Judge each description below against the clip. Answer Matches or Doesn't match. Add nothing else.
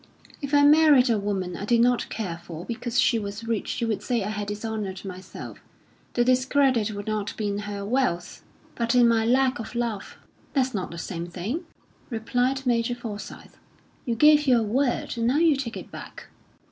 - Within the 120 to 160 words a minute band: Doesn't match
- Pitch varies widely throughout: Doesn't match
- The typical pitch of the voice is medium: Doesn't match